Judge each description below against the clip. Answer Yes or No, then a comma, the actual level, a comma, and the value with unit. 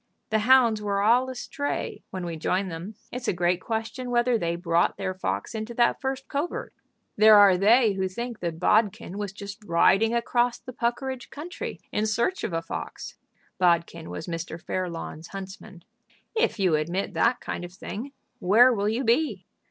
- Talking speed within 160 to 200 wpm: Yes, average, 175 wpm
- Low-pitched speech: No, high, 210 Hz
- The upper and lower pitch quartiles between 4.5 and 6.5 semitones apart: Yes, average, 4.9 semitones